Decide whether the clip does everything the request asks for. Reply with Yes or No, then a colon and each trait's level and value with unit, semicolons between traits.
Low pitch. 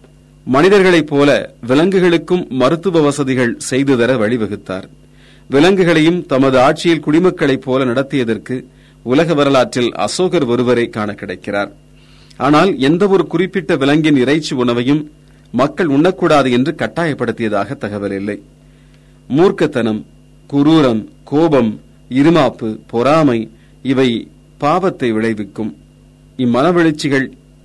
Yes: low, 130 Hz